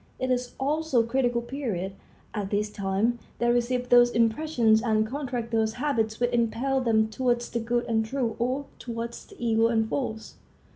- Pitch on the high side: Yes, high, 235 Hz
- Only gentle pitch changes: Yes, narrow, 2.2 semitones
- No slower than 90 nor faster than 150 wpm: No, average, 175 wpm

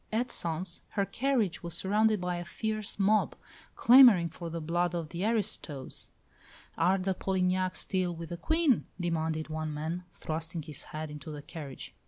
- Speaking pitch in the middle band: Yes, medium, 175 Hz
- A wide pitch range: No, average, 3.7 semitones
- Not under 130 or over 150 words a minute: No, average, 165 wpm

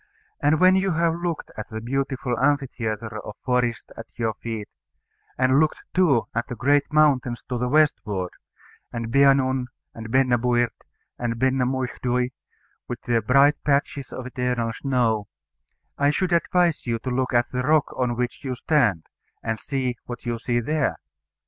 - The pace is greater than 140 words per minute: Yes, average, 160 wpm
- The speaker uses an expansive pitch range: No, average, 3.1 semitones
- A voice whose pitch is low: Yes, low, 125 Hz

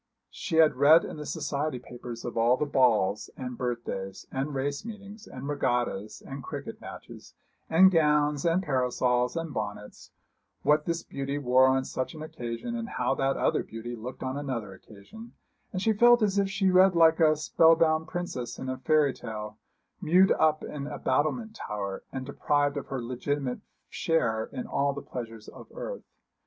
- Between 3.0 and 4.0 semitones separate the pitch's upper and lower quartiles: No, average, 4.8 semitones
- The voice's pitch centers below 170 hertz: Yes, medium, 140 Hz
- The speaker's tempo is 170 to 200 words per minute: Yes, average, 175 wpm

